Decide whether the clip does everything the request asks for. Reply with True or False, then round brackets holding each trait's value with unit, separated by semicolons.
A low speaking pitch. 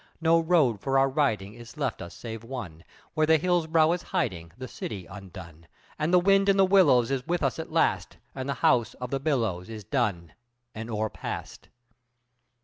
True (125 Hz)